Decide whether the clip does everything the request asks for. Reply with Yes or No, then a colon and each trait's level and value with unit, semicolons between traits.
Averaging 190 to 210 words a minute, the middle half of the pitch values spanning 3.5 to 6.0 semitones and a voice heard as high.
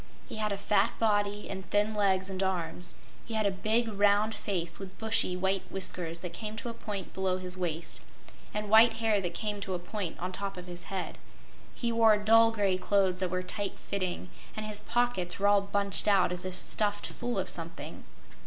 No: fast, 205 wpm; narrow, 2.6 semitones; high, 200 Hz